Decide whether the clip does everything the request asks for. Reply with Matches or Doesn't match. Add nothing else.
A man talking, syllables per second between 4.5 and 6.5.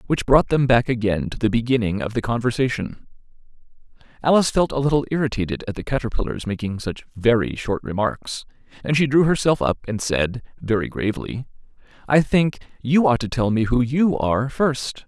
Matches